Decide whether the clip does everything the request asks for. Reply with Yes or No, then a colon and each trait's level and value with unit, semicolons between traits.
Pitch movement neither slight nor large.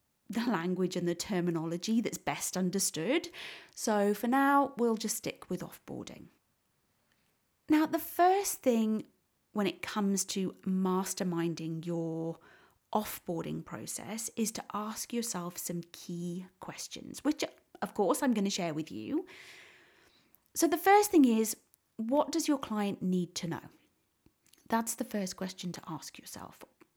No: wide, 6.7 semitones